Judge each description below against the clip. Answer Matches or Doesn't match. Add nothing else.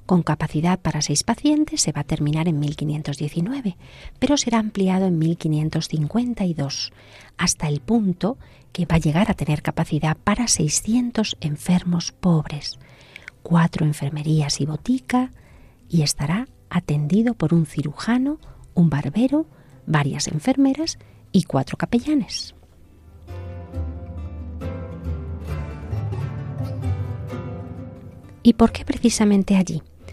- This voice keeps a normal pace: Doesn't match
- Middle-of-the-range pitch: Matches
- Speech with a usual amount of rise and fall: Doesn't match